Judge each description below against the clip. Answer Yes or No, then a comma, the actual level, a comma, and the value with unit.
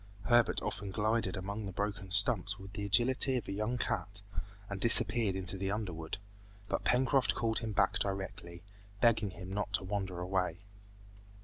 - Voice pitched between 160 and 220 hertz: No, low, 100 Hz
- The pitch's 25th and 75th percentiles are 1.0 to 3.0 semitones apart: Yes, narrow, 2.6 semitones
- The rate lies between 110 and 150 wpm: No, average, 165 wpm